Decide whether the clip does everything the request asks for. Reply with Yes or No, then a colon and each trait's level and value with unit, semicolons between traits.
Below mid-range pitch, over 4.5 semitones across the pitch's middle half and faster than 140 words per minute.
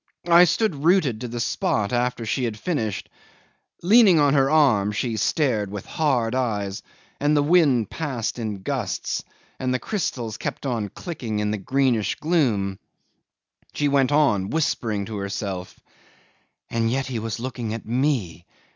Yes: low, 120 Hz; wide, 5.4 semitones; average, 150 wpm